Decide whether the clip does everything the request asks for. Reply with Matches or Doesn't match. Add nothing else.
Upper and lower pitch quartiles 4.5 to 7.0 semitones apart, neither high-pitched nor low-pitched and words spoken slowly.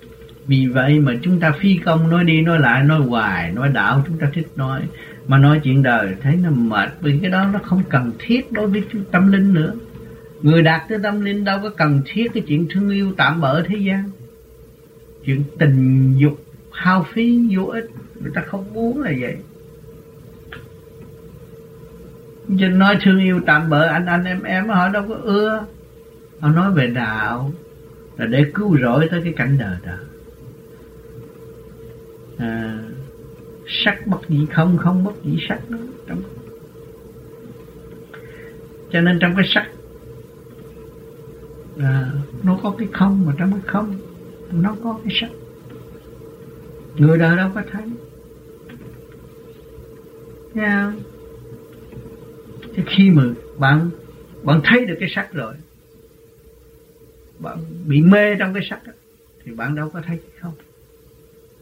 Matches